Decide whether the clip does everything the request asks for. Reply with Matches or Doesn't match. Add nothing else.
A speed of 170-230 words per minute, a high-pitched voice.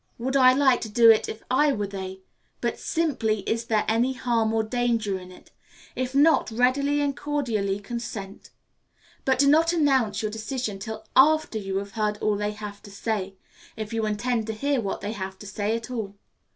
Matches